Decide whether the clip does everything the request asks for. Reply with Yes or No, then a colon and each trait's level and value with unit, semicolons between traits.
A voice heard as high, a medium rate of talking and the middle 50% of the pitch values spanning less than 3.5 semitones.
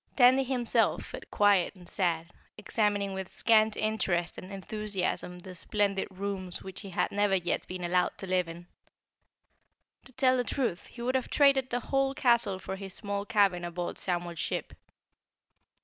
No: high, 200 Hz; average, 165 wpm; average, 4.1 semitones